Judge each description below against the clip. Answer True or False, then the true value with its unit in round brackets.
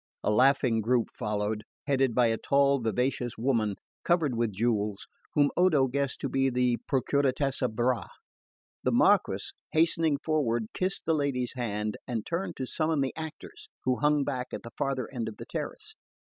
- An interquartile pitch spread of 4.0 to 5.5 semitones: False (3.5 semitones)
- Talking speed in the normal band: True (165 wpm)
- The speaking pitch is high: False (130 Hz)